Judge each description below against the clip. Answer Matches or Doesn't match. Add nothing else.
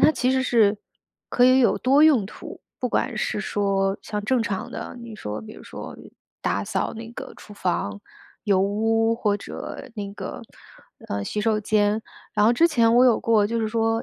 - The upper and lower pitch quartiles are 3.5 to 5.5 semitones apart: Doesn't match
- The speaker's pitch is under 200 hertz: Doesn't match